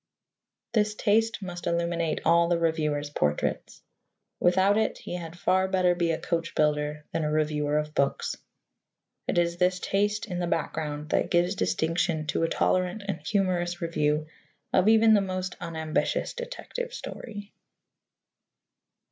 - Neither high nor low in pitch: Yes, medium, 175 Hz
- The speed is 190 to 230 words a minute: No, average, 145 wpm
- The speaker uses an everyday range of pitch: Yes, average, 3.4 semitones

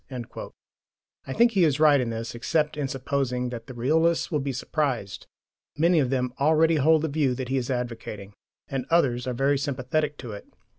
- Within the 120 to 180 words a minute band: No, average, 190 wpm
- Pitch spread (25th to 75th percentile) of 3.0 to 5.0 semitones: Yes, average, 3.7 semitones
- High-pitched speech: No, low, 135 Hz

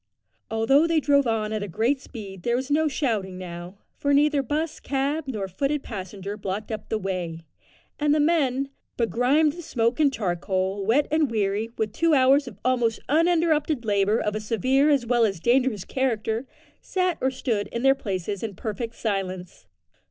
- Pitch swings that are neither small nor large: No, wide, 5.7 semitones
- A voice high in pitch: Yes, high, 235 Hz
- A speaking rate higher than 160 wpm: Yes, average, 175 wpm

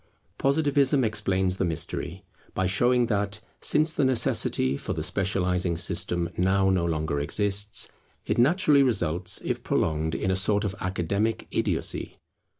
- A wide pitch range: No, average, 5.0 semitones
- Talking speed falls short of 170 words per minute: Yes, average, 140 wpm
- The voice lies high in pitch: No, very low, 95 Hz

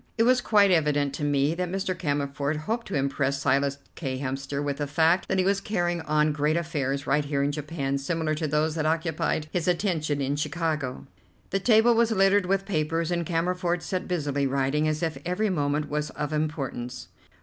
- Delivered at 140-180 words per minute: No, average, 195 wpm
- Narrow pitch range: No, average, 3.8 semitones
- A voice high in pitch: No, medium, 155 Hz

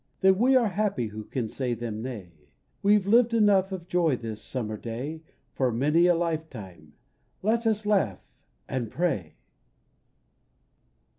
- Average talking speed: Yes, average, 150 wpm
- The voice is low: No, medium, 160 Hz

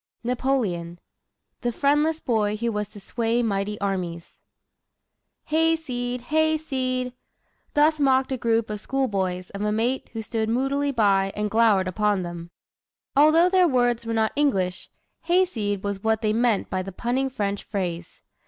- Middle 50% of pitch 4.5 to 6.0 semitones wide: Yes, average, 4.8 semitones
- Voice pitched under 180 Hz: No, high, 230 Hz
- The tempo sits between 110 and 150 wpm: Yes, average, 145 wpm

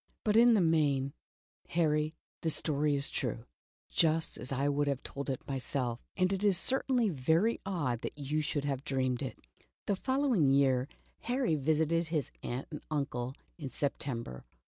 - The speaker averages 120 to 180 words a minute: No, average, 190 wpm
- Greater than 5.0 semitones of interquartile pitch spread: No, average, 3.8 semitones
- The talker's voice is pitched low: No, medium, 150 Hz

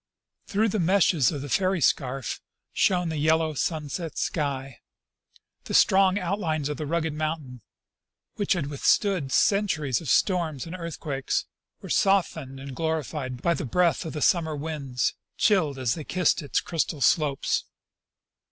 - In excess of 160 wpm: No, average, 145 wpm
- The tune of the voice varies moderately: Yes, average, 4.1 semitones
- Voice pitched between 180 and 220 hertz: No, medium, 155 Hz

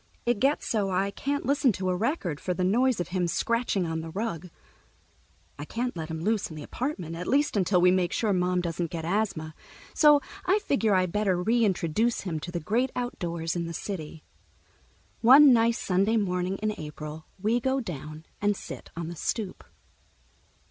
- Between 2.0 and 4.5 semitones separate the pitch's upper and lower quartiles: No, wide, 5.4 semitones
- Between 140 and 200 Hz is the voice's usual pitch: Yes, high, 190 Hz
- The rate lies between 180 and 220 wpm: Yes, average, 185 wpm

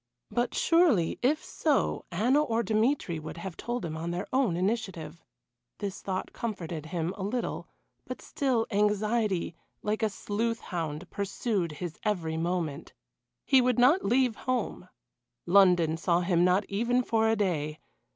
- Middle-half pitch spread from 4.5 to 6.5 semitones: Yes, wide, 5.4 semitones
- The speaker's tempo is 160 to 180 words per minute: No, average, 150 wpm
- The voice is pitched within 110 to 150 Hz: No, high, 200 Hz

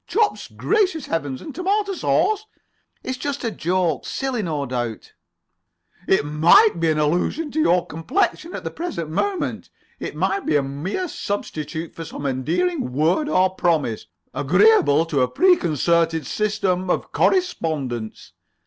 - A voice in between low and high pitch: Yes, medium, 175 Hz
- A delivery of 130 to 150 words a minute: Yes, average, 145 wpm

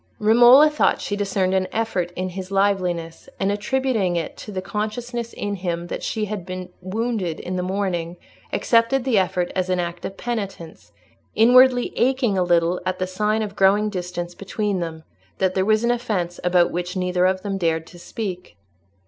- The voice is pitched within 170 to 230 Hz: Yes, high, 190 Hz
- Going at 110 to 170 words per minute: No, average, 180 wpm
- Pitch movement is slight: No, average, 3.3 semitones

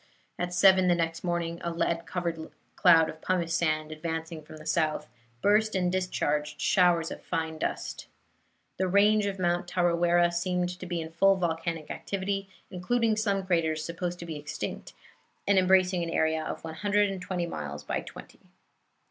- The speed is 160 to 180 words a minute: Yes, average, 170 wpm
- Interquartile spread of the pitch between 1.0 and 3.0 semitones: Yes, narrow, 2.4 semitones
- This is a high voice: No, medium, 175 Hz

